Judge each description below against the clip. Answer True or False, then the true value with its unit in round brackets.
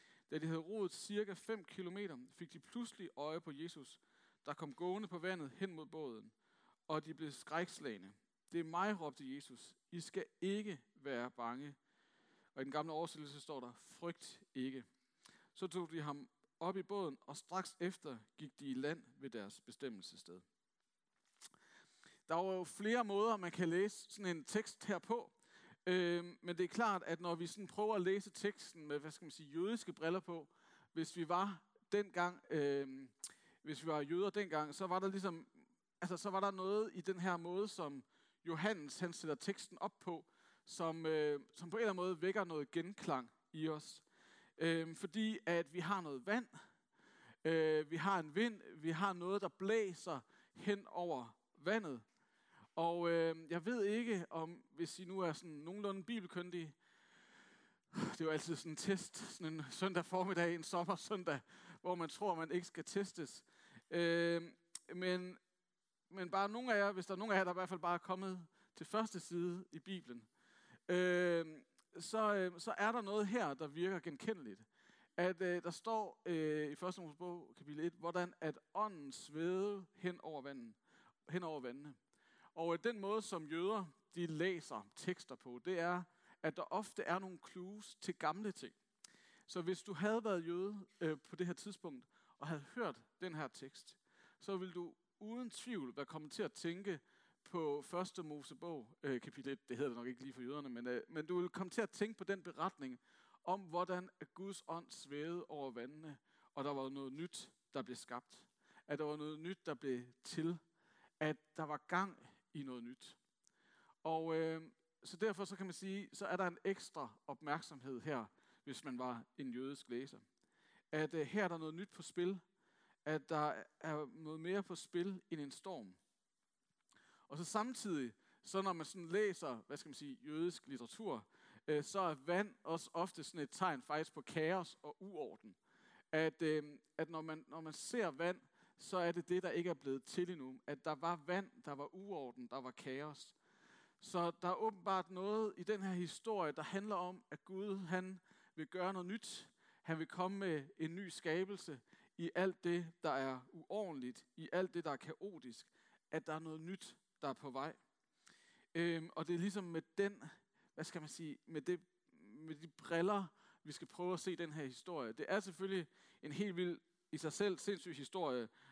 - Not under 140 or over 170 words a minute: False (190 wpm)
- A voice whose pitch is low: False (175 Hz)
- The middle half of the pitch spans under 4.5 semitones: True (3.8 semitones)